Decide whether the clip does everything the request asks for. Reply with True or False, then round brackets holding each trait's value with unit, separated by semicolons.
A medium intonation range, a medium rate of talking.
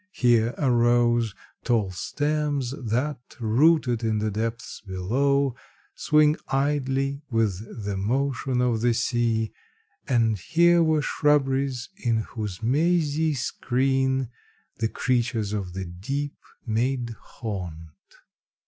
False (3.9 semitones; 105 wpm)